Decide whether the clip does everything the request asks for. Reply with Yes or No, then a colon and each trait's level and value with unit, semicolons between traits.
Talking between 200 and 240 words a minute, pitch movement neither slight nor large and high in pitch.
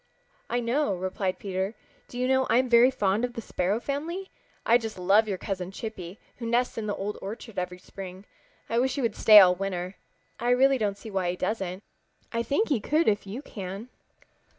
Yes: fast, 205 wpm; average, 4.3 semitones; high, 215 Hz